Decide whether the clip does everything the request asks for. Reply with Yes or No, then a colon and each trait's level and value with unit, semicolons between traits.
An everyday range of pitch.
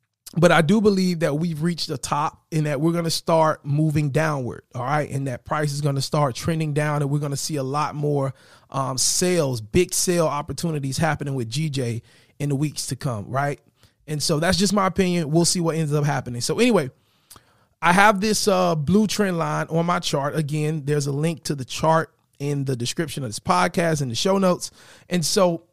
Yes: average, 3.6 semitones